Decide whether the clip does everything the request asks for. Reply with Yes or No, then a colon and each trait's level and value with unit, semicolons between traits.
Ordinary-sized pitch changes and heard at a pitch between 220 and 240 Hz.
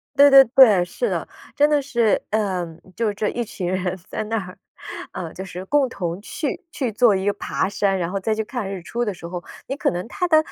No: average, 4.9 semitones; high, 210 Hz